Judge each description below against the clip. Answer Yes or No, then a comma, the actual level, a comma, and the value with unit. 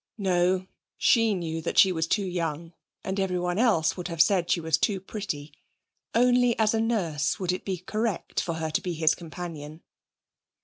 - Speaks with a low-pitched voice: No, medium, 180 Hz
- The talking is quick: No, average, 180 wpm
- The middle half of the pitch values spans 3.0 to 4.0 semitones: Yes, average, 3.7 semitones